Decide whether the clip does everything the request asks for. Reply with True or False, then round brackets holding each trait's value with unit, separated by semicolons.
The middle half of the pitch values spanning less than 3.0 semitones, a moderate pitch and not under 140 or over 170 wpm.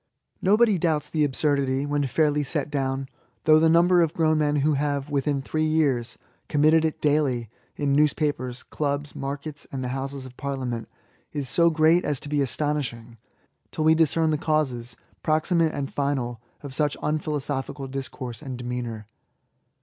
True (2.6 semitones; 145 Hz; 165 wpm)